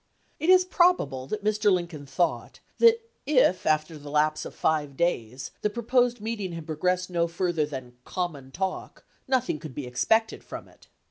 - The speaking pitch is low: No, medium, 175 Hz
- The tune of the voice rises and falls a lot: Yes, wide, 6.6 semitones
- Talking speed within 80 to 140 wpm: No, average, 170 wpm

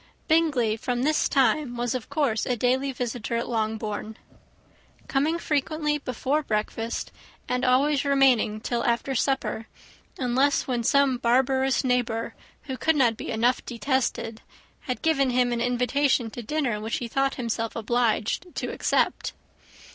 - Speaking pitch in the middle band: No, very high, 250 Hz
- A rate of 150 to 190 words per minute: No, average, 140 wpm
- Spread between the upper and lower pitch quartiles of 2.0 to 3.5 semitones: Yes, average, 2.8 semitones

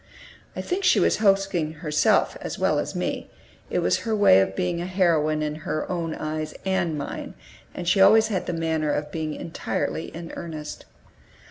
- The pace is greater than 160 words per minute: Yes, average, 180 wpm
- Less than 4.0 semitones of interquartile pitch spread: Yes, average, 3.6 semitones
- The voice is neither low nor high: Yes, medium, 165 Hz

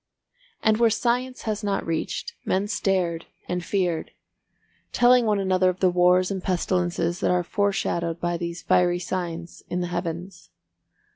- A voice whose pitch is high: No, medium, 180 Hz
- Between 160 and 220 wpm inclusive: No, average, 150 wpm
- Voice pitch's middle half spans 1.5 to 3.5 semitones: Yes, narrow, 2.5 semitones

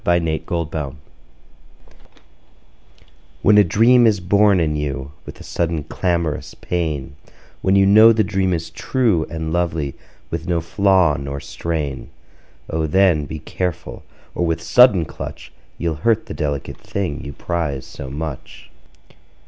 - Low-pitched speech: Yes, very low, 85 Hz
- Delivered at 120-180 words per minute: Yes, average, 150 wpm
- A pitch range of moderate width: Yes, average, 4.2 semitones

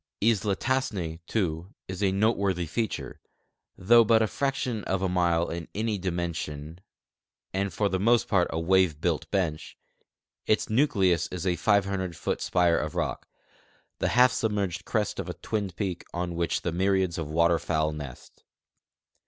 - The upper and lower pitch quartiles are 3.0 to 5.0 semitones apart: Yes, average, 3.6 semitones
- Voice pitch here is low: Yes, very low, 95 Hz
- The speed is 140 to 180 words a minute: Yes, average, 155 wpm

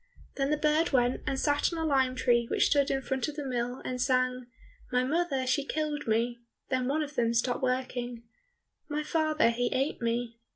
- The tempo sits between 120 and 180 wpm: No, average, 200 wpm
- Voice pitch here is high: Yes, very high, 260 Hz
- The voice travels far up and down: No, average, 3.2 semitones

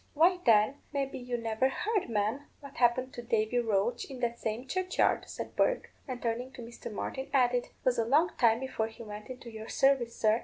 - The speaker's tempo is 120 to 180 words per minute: No, average, 200 wpm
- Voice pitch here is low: No, high, 245 Hz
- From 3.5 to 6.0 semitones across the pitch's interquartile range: No, average, 2.9 semitones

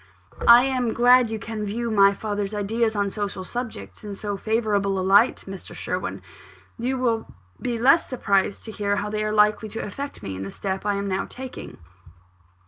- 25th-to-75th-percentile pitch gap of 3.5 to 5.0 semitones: No, average, 2.8 semitones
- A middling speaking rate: Yes, average, 190 wpm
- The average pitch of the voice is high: Yes, high, 210 Hz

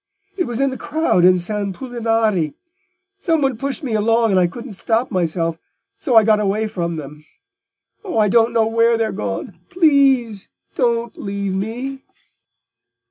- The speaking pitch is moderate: No, high, 225 Hz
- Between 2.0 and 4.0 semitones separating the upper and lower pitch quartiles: No, average, 5.2 semitones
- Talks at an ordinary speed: Yes, average, 150 wpm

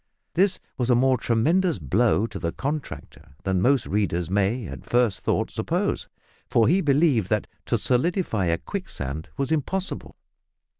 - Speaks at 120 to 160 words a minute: Yes, average, 150 wpm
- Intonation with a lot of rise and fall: Yes, wide, 7.6 semitones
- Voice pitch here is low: Yes, low, 120 Hz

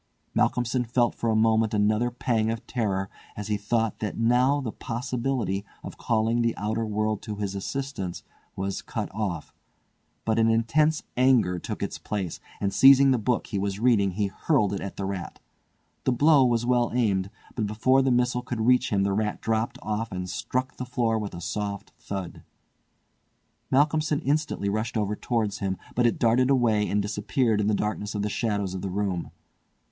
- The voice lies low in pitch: Yes, low, 110 Hz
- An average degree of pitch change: Yes, average, 3.4 semitones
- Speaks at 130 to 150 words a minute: No, average, 185 wpm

